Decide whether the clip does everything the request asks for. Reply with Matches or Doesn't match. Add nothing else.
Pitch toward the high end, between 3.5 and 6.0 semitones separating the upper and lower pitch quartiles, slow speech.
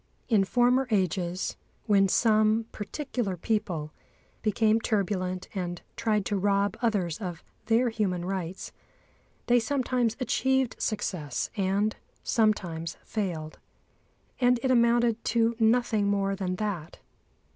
Matches